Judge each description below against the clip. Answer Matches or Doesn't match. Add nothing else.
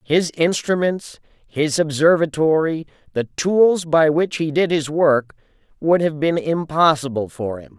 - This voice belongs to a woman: Doesn't match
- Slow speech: Matches